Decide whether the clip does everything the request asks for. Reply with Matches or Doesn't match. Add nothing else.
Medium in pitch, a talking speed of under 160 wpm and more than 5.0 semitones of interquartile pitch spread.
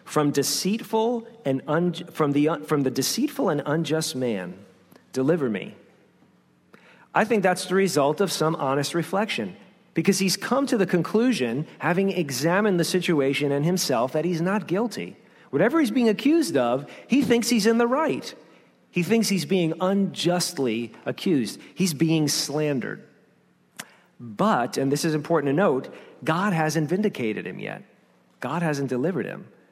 Matches